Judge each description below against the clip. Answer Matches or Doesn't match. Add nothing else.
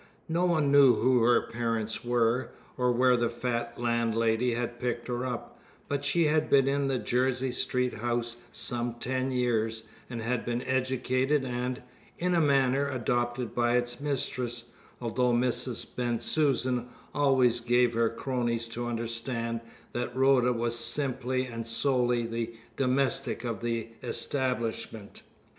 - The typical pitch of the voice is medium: Doesn't match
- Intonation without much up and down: Matches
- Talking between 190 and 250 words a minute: Doesn't match